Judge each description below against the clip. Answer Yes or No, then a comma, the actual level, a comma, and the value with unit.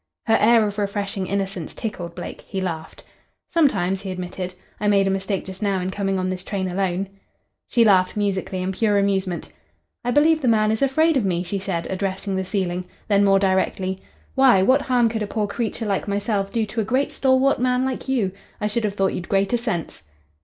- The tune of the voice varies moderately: Yes, average, 3.0 semitones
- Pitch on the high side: Yes, high, 200 Hz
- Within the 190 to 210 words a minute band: Yes, fast, 205 wpm